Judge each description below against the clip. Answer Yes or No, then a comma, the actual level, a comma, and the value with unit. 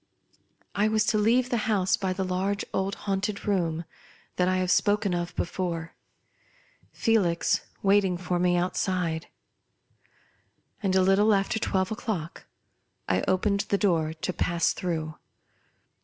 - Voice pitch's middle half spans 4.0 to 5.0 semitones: No, narrow, 2.6 semitones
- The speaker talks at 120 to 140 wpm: Yes, slow, 135 wpm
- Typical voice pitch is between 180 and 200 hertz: Yes, high, 190 Hz